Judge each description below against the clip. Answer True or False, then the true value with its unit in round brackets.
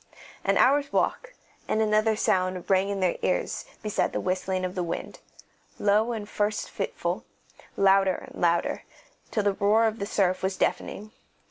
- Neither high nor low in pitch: False (200 Hz)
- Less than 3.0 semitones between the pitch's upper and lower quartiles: True (2.5 semitones)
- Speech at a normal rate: True (165 wpm)